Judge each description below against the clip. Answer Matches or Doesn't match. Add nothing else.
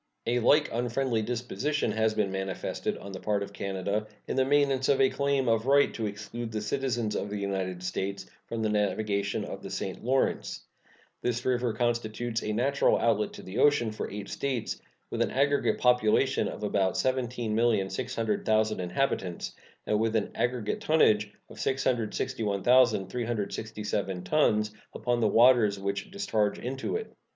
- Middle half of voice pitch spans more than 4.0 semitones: Doesn't match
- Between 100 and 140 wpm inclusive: Doesn't match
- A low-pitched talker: Matches